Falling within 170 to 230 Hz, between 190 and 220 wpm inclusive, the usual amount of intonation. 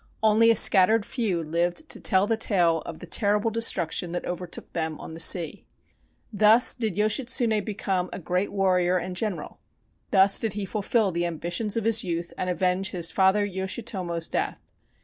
No: high, 190 Hz; average, 170 wpm; average, 3.5 semitones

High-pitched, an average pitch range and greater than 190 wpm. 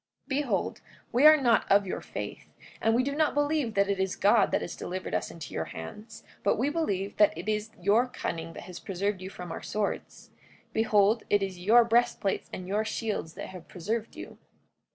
Yes: high, 210 Hz; average, 3.8 semitones; average, 200 wpm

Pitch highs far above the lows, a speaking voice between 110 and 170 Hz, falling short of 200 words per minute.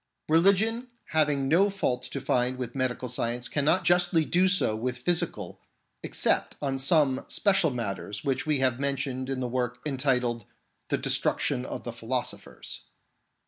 No: average, 4.6 semitones; low, 135 Hz; average, 145 wpm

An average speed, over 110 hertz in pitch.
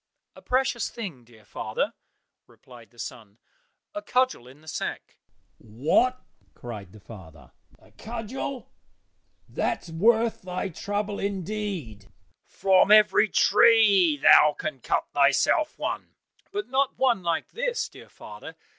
No: slow, 125 wpm; high, 190 Hz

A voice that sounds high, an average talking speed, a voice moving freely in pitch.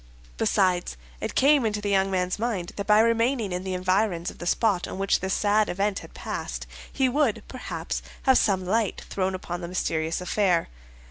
No: high, 195 Hz; average, 190 wpm; average, 3.3 semitones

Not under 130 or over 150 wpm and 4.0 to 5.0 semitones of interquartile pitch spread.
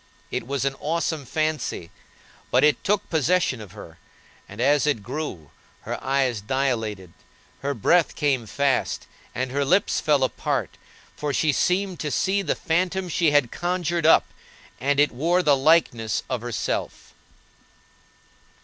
Yes: average, 145 wpm; average, 4.7 semitones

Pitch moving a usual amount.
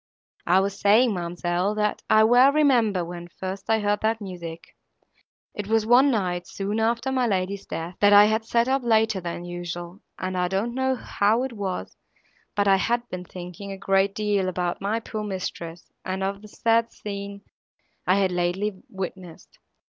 Yes: average, 3.3 semitones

